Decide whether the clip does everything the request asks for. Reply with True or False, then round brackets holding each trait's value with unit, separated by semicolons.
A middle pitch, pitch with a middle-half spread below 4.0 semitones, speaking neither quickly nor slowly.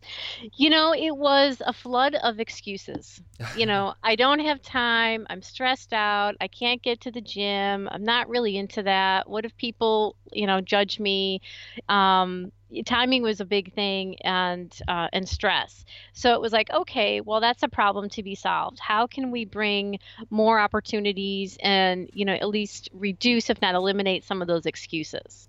False (210 Hz; 3.6 semitones; 180 wpm)